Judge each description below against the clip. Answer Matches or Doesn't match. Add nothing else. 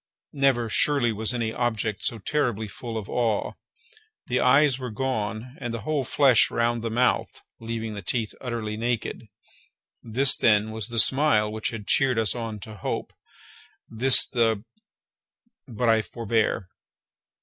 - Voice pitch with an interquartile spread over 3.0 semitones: Doesn't match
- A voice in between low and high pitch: Doesn't match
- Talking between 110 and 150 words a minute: Matches